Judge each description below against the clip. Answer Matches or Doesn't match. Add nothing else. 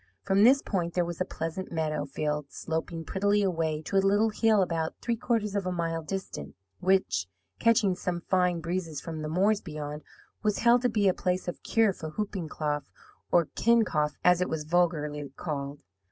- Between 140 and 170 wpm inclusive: Doesn't match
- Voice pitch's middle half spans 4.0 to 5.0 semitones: Matches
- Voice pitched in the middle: Matches